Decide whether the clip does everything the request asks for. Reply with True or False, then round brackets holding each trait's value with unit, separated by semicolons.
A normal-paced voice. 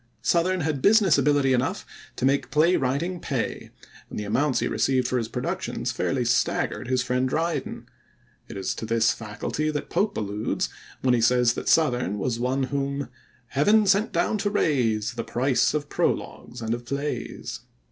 True (170 wpm)